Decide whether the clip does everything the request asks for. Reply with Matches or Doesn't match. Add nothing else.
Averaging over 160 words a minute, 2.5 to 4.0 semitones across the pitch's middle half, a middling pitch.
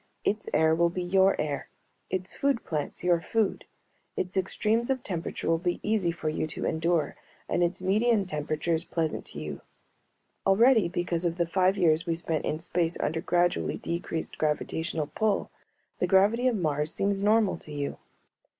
Matches